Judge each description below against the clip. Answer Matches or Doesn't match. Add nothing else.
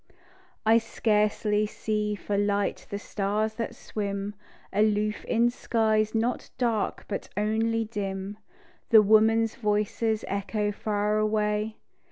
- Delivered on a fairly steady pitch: Matches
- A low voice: Doesn't match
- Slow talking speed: Matches